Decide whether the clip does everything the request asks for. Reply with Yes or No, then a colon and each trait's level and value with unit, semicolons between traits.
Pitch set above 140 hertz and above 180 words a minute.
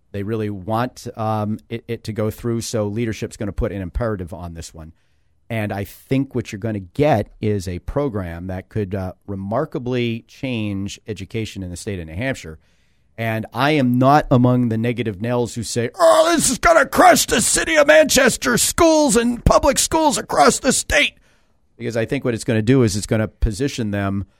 No: low, 115 Hz; fast, 205 wpm